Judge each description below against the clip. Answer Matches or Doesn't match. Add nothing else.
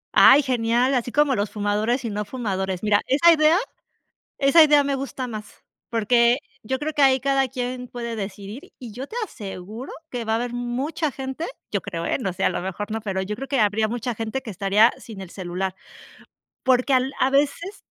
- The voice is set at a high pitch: Matches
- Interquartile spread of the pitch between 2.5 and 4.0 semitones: Doesn't match